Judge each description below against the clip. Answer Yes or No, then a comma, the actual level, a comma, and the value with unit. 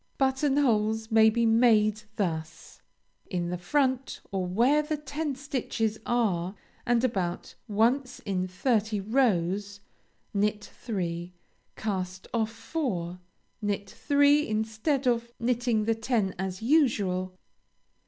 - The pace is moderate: No, slow, 115 wpm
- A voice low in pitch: No, high, 220 Hz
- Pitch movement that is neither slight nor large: Yes, average, 4.7 semitones